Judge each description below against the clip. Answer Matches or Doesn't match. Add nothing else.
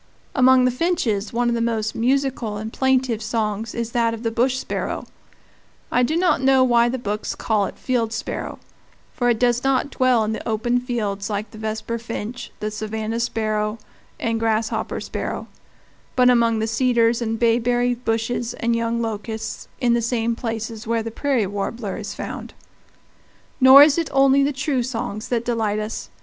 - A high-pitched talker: Matches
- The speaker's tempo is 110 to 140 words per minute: Doesn't match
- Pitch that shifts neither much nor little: Doesn't match